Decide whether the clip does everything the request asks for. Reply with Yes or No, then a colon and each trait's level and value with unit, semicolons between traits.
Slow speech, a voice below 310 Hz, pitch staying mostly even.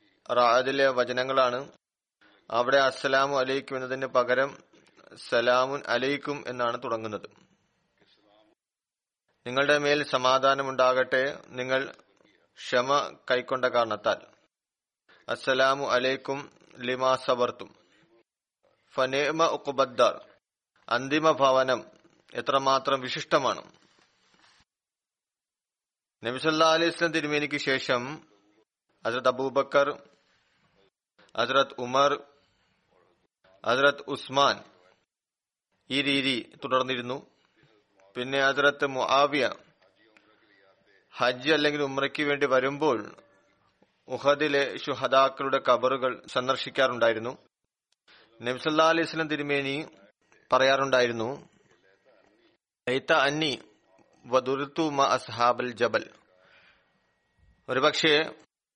Yes: slow, 55 wpm; low, 135 Hz; narrow, 2.1 semitones